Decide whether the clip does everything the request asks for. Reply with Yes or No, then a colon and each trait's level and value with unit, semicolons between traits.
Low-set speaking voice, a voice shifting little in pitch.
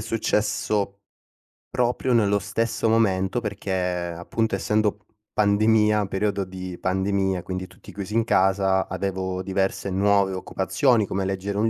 Yes: low, 100 Hz; narrow, 2.0 semitones